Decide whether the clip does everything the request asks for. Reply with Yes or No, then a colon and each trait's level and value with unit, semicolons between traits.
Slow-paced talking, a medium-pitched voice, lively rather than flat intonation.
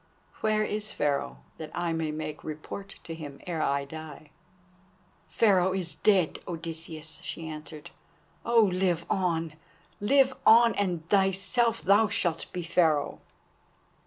No: slow, 130 wpm; medium, 170 Hz; average, 4.2 semitones